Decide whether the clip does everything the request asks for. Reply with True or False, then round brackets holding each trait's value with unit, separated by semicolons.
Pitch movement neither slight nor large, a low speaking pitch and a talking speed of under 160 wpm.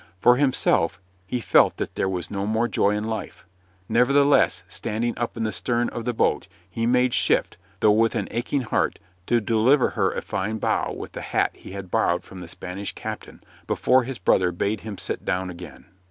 False (4.0 semitones; 110 Hz; 195 wpm)